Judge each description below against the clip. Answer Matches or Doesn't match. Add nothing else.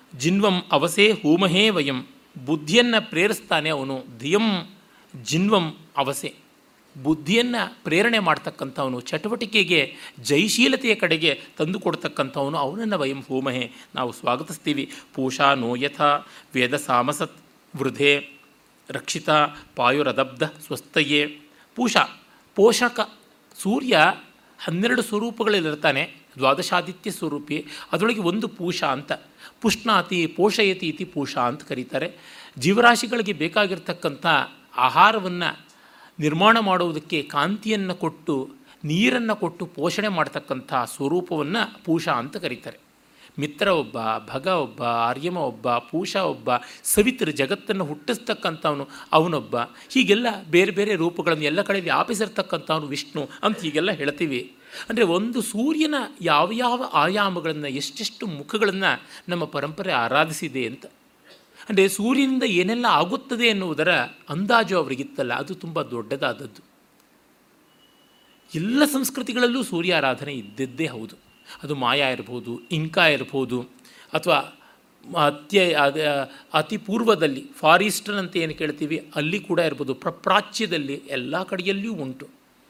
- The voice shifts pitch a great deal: Matches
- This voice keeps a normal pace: Matches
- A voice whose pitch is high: Doesn't match